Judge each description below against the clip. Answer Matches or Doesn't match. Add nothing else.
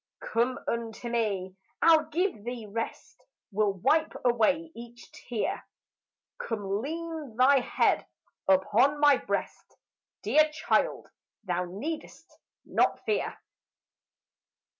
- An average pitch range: Doesn't match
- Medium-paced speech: Doesn't match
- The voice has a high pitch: Matches